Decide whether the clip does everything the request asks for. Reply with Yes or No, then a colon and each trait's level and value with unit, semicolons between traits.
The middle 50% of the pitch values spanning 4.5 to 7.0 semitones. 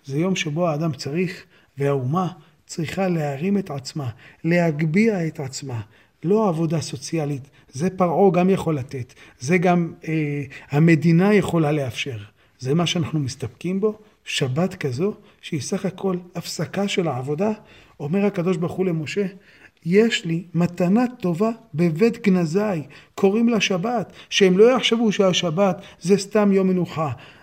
Yes: average, 4.8 semitones